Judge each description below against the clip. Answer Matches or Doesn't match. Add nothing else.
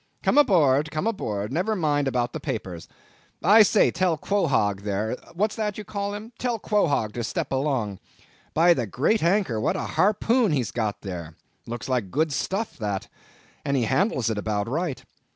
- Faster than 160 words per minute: Matches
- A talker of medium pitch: Matches